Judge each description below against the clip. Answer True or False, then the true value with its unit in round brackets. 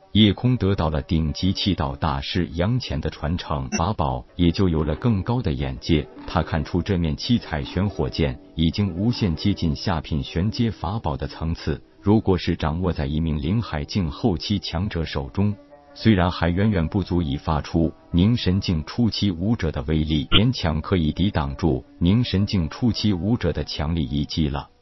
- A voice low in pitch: True (85 Hz)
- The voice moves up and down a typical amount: True (4.7 semitones)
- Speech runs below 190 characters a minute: False (265 characters per minute)